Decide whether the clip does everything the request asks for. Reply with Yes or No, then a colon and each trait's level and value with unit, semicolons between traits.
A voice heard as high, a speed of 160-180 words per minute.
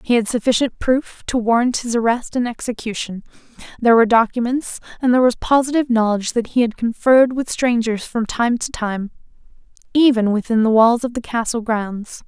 Yes: high, 235 Hz; average, 175 wpm